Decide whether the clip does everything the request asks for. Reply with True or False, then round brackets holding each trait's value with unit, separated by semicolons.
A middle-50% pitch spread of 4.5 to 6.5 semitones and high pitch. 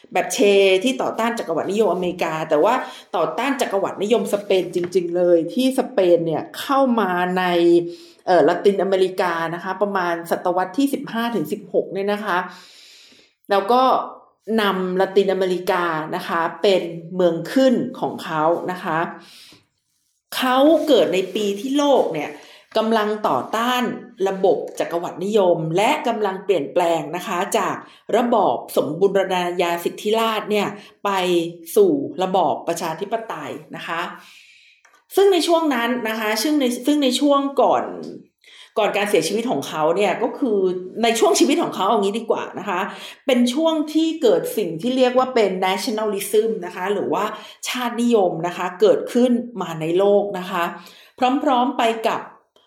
True (5.3 semitones; 200 Hz)